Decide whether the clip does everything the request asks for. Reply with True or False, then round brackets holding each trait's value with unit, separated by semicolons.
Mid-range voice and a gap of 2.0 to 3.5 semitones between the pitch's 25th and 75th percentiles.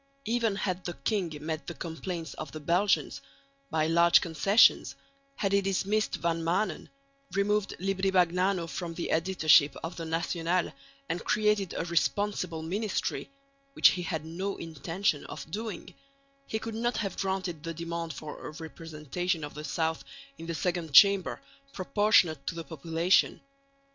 True (175 Hz; 3.2 semitones)